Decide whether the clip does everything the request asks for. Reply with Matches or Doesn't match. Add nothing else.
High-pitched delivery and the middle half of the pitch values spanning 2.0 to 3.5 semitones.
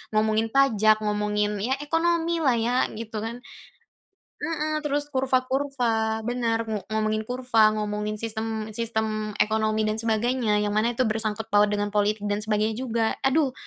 Matches